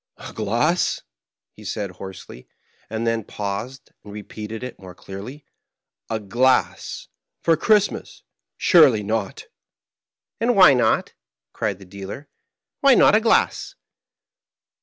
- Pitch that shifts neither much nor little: No, wide, 6.3 semitones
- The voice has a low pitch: Yes, low, 110 Hz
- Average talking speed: No, slow, 130 wpm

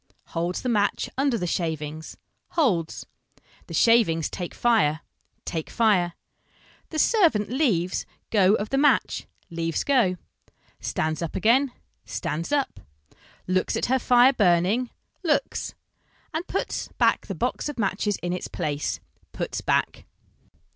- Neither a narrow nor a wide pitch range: No, wide, 7.0 semitones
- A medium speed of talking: No, slow, 130 wpm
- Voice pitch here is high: Yes, high, 205 Hz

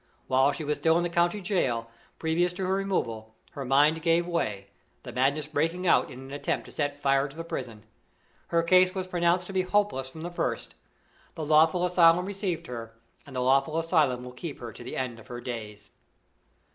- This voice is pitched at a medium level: Yes, medium, 155 Hz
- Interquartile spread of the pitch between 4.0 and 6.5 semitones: Yes, average, 5.2 semitones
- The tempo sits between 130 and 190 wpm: No, fast, 205 wpm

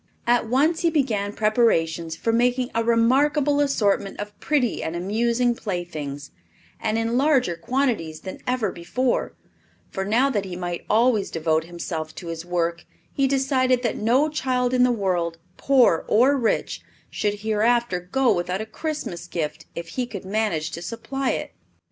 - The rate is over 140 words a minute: Yes, average, 160 wpm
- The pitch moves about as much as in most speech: No, wide, 6.3 semitones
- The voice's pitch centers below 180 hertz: No, high, 220 Hz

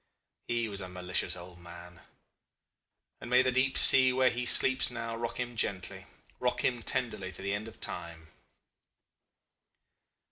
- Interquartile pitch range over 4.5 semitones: Yes, wide, 5.4 semitones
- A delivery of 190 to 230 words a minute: No, average, 150 wpm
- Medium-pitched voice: No, low, 115 Hz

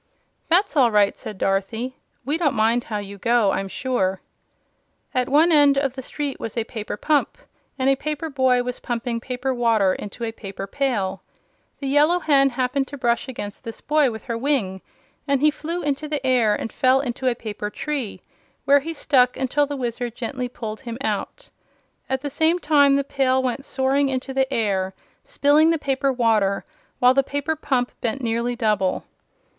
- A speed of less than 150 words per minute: No, average, 185 wpm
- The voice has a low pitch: No, very high, 255 Hz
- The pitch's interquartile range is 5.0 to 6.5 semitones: No, average, 3.7 semitones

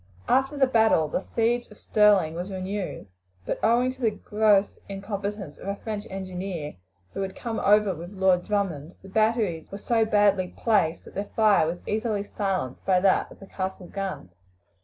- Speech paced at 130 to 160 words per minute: No, average, 180 wpm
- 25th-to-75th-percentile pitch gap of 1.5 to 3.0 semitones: Yes, narrow, 2.6 semitones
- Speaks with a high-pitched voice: Yes, high, 200 Hz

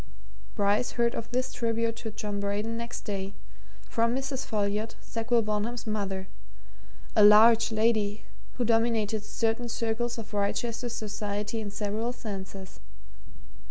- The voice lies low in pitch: No, high, 220 Hz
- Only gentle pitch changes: Yes, narrow, 2.1 semitones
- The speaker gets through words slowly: Yes, slow, 125 wpm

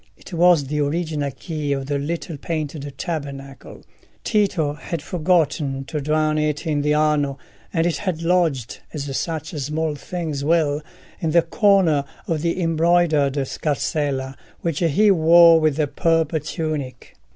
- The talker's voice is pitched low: No, medium, 155 Hz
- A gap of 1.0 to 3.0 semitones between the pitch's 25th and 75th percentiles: Yes, narrow, 2.6 semitones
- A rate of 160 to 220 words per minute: No, average, 145 wpm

